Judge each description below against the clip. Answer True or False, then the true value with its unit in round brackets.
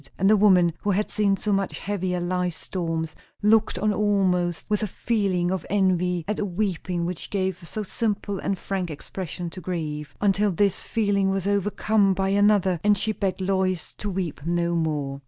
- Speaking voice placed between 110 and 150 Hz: False (190 Hz)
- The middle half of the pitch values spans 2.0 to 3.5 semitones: True (2.6 semitones)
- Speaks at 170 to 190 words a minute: True (180 wpm)